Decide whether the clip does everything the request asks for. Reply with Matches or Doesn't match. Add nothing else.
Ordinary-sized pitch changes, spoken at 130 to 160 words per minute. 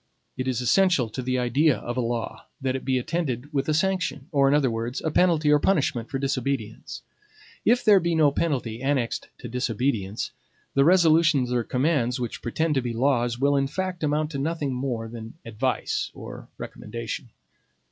Doesn't match